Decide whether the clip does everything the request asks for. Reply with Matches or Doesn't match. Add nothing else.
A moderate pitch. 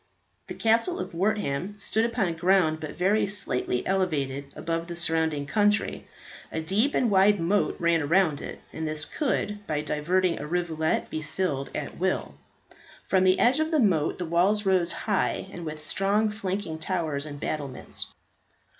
Matches